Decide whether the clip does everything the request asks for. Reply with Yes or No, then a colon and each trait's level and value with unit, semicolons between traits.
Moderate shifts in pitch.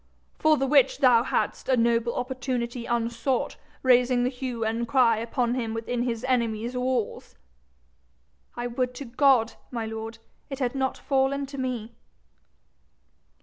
No: narrow, 2.0 semitones